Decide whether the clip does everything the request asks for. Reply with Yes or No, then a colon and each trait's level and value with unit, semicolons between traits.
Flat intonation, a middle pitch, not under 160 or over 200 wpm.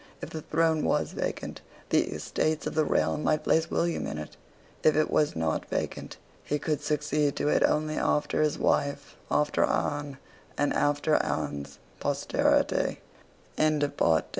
No: narrow, 1.3 semitones; medium, 150 Hz; average, 145 wpm